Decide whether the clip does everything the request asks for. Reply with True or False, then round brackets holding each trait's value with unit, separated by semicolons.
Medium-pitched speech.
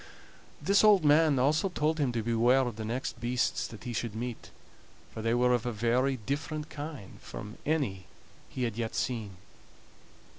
False (125 Hz)